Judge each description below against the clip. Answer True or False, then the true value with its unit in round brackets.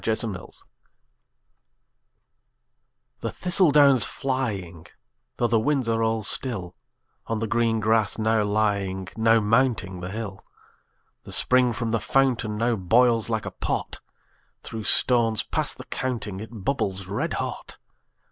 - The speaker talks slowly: True (130 wpm)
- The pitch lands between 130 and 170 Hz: False (115 Hz)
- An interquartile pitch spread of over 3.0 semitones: False (2.7 semitones)